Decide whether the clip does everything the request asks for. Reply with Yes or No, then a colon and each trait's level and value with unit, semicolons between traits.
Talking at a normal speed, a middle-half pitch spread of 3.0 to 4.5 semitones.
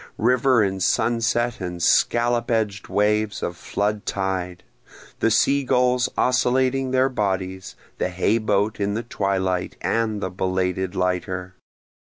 No: slow, 130 wpm; average, 4.1 semitones